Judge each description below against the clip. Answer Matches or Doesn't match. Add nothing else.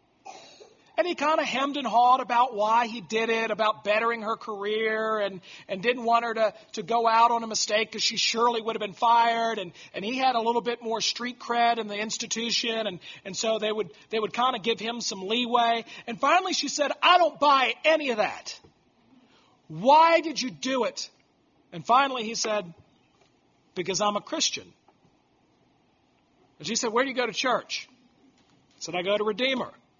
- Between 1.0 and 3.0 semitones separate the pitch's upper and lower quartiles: Matches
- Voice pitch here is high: Matches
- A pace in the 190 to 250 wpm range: Matches